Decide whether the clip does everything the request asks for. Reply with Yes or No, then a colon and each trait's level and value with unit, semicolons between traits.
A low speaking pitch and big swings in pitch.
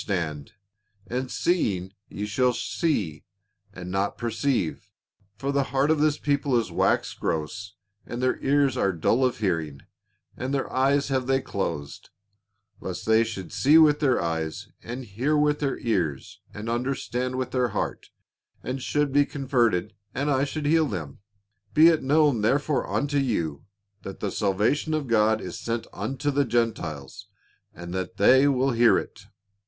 Yes: low, 125 Hz; wide, 6.1 semitones